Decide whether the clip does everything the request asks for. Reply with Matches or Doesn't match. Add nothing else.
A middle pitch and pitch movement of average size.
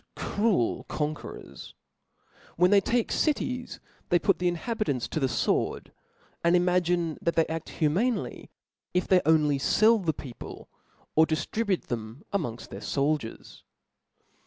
Matches